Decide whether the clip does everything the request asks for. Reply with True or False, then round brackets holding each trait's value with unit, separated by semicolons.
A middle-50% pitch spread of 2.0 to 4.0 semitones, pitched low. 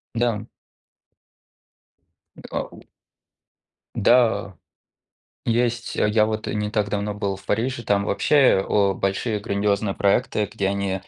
True (2.4 semitones; 105 Hz)